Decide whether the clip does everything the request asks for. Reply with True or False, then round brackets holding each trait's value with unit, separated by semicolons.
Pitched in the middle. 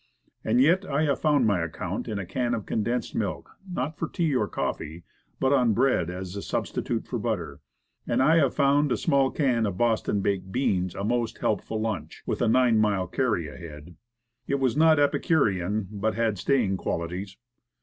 False (115 Hz)